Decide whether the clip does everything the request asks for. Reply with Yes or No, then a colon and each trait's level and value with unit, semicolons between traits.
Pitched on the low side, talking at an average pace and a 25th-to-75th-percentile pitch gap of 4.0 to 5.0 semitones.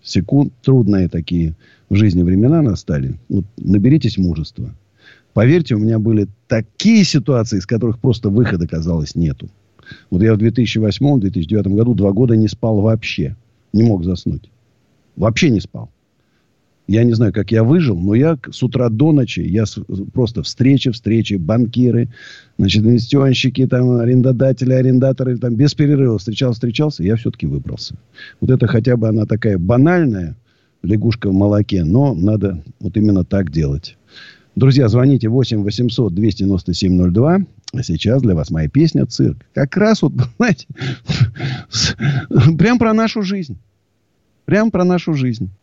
Yes: low, 115 Hz; average, 145 wpm; average, 4.7 semitones